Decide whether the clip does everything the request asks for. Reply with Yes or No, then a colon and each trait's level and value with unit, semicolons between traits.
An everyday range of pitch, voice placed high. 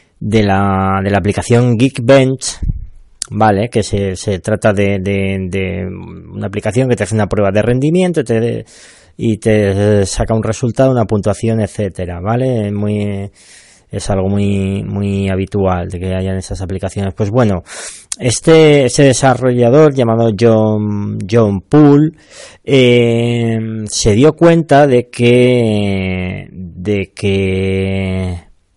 No: average, 3.5 semitones; low, 105 Hz